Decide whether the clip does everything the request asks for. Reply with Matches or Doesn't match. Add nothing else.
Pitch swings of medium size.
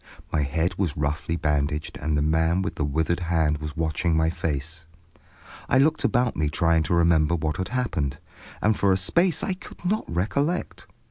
Matches